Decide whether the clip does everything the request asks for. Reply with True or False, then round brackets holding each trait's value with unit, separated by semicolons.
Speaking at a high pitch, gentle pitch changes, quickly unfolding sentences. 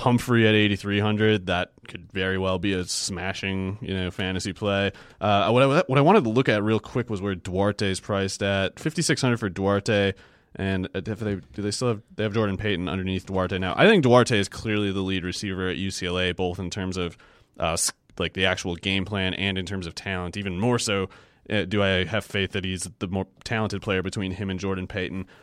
False (95 Hz; 2.1 semitones; 225 wpm)